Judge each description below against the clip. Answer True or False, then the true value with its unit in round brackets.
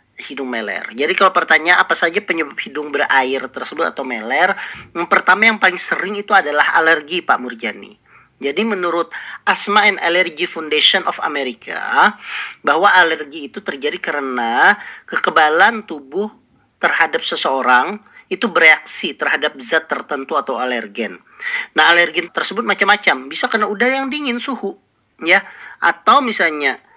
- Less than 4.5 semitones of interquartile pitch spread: False (4.9 semitones)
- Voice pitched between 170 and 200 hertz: True (190 Hz)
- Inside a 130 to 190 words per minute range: True (135 wpm)